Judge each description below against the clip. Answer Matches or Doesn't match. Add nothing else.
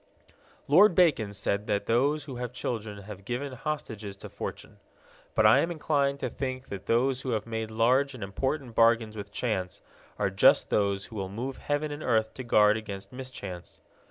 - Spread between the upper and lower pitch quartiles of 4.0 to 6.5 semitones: Matches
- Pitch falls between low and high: Doesn't match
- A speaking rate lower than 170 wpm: Doesn't match